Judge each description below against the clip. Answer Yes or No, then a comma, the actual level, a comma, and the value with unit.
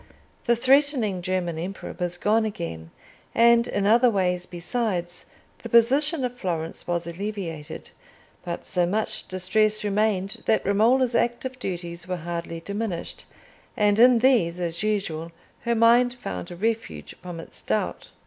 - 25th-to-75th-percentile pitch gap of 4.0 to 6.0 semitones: Yes, average, 5.1 semitones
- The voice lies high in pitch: Yes, high, 200 Hz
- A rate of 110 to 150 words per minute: Yes, average, 140 wpm